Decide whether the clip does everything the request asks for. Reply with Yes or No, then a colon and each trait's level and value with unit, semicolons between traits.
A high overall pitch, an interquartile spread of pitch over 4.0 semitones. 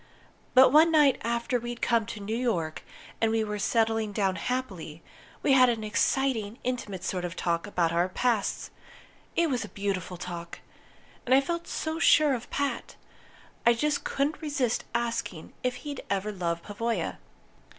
Yes: high, 230 Hz; average, 4.8 semitones